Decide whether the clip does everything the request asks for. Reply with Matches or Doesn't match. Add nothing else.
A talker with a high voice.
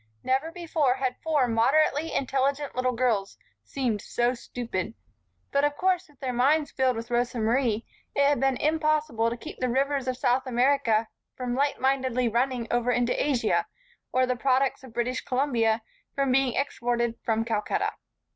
Matches